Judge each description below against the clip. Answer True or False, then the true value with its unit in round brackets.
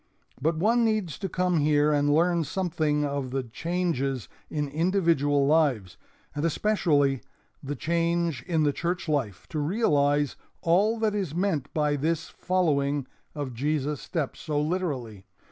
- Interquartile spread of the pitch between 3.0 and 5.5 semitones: True (3.4 semitones)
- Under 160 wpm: True (145 wpm)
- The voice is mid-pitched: True (150 Hz)